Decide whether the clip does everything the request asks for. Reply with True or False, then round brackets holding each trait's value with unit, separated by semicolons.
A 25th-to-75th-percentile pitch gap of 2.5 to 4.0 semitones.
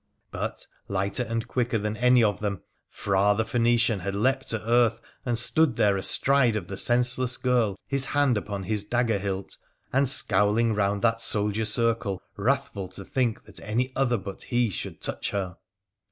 True (3.3 semitones)